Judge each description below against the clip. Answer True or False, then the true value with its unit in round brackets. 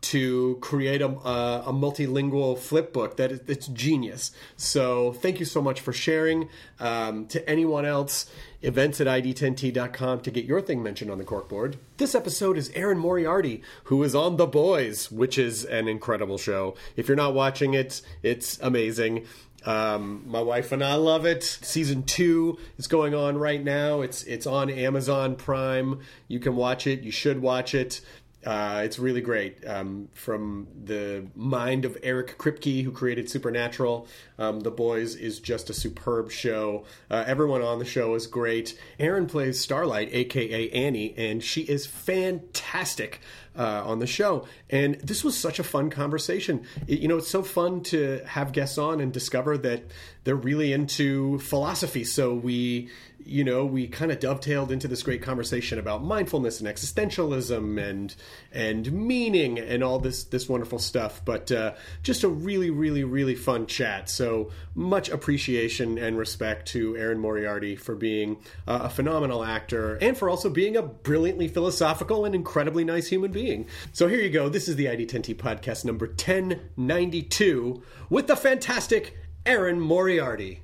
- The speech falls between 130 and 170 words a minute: True (165 wpm)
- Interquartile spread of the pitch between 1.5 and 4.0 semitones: False (4.5 semitones)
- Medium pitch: False (130 Hz)